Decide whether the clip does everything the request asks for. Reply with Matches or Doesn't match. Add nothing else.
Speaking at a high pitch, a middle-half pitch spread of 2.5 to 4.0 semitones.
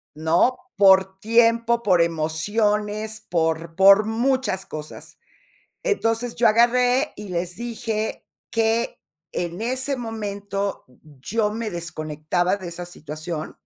Doesn't match